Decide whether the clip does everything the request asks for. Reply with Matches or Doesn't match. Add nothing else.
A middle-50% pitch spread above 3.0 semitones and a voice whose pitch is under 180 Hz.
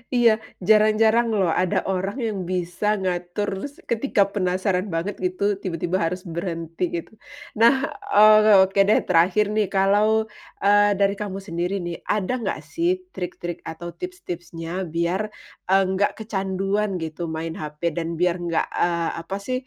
Doesn't match